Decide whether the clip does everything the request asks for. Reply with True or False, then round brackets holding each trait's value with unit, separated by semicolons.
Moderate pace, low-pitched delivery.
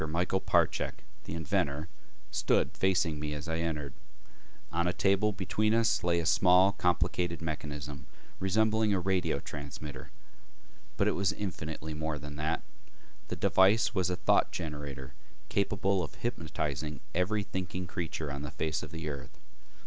True (150 wpm; 85 Hz)